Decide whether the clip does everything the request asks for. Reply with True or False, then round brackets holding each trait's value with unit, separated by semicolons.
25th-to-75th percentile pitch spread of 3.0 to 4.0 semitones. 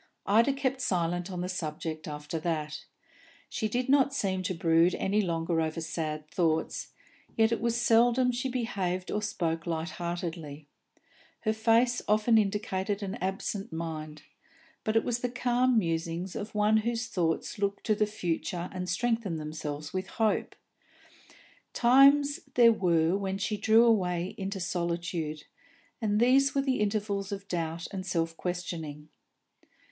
False (5.2 semitones)